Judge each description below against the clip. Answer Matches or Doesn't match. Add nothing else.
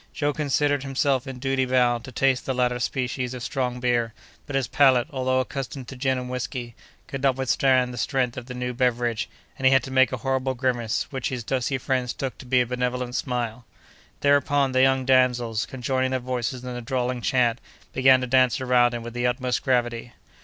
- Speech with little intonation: Matches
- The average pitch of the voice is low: Matches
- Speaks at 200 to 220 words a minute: Matches